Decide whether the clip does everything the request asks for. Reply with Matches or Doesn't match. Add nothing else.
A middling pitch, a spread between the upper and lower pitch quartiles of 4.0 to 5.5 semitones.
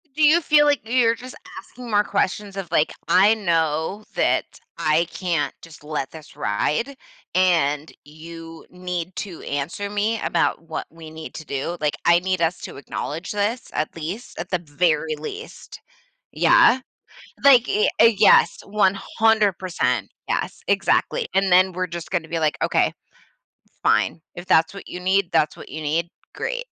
Matches